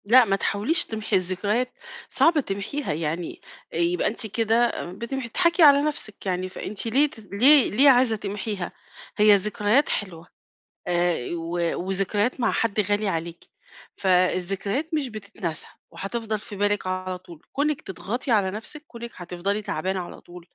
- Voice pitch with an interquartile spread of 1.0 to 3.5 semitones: No, average, 4.3 semitones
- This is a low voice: No, high, 205 Hz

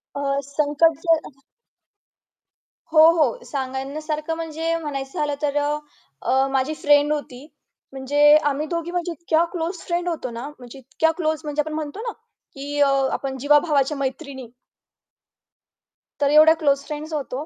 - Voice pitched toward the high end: Yes, very high, 295 Hz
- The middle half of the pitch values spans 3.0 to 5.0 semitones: No, narrow, 2.4 semitones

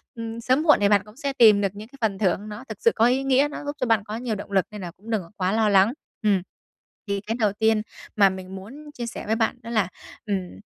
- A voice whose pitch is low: No, high, 215 Hz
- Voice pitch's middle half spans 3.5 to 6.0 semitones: No, average, 3.0 semitones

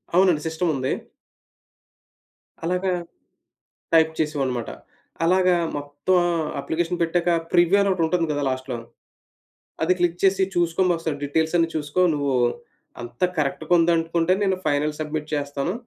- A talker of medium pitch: Yes, medium, 165 Hz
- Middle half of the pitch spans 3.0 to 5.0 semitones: Yes, average, 3.3 semitones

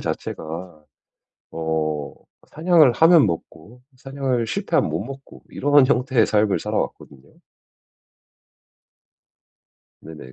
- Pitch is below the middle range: Yes, low, 110 Hz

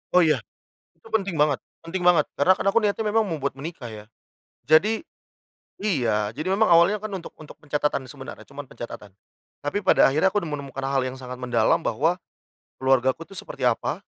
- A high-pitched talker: No, medium, 150 Hz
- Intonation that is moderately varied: No, wide, 5.9 semitones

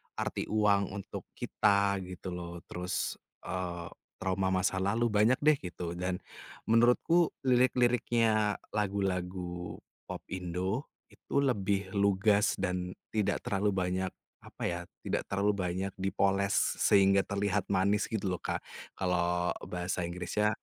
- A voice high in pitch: No, very low, 95 Hz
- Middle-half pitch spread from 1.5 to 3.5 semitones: Yes, narrow, 2.4 semitones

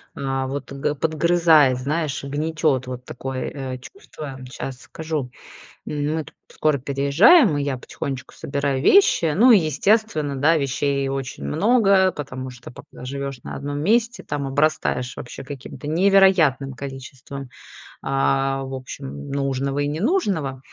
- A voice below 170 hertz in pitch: Yes, medium, 140 Hz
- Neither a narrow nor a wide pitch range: Yes, average, 3.1 semitones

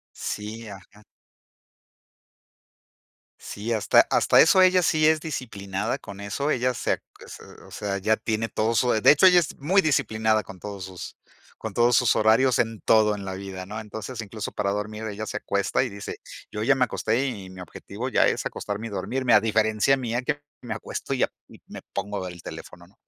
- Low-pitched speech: Yes, low, 110 Hz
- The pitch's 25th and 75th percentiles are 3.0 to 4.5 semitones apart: Yes, average, 3.6 semitones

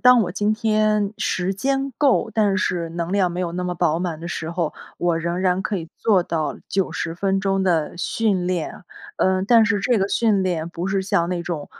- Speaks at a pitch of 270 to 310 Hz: No, medium, 185 Hz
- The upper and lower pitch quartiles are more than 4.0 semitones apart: No, average, 3.2 semitones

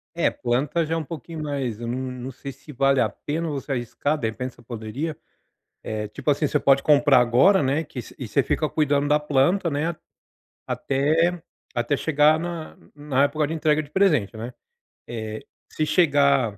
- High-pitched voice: No, medium, 140 Hz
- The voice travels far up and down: No, average, 3.5 semitones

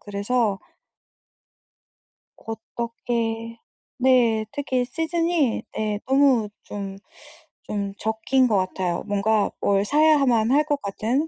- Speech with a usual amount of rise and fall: Yes, average, 4.4 semitones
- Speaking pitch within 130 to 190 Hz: No, high, 230 Hz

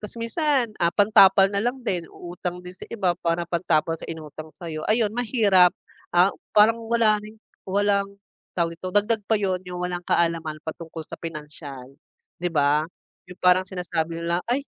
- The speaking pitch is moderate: Yes, medium, 180 Hz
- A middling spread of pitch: Yes, average, 3.8 semitones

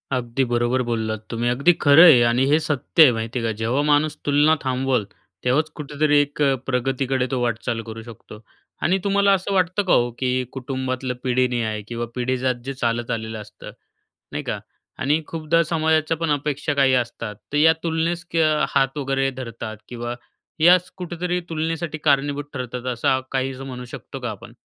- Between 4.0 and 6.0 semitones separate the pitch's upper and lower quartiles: Yes, average, 4.3 semitones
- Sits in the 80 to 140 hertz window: Yes, low, 135 Hz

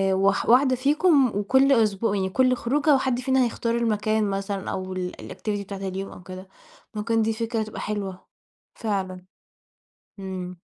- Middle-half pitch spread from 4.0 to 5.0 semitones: Yes, average, 4.3 semitones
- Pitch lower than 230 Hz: Yes, high, 215 Hz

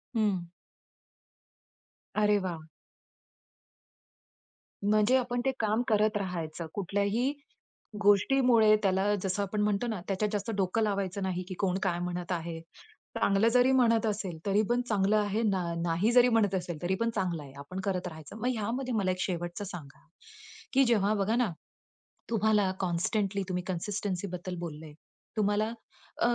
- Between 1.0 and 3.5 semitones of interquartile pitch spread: Yes, average, 3.1 semitones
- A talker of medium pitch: No, high, 200 Hz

